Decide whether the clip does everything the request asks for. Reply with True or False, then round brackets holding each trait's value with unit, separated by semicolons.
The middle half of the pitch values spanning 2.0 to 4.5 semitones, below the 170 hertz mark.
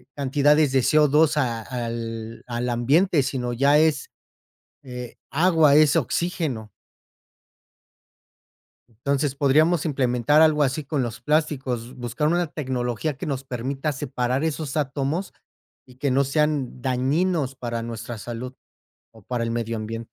True (3.8 semitones; 135 Hz)